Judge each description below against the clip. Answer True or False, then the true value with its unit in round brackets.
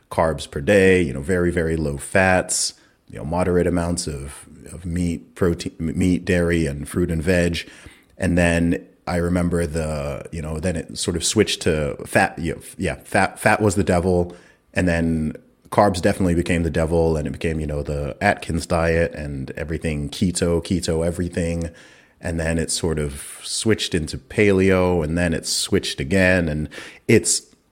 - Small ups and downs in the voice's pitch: True (2.1 semitones)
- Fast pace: False (175 wpm)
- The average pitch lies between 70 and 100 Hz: True (85 Hz)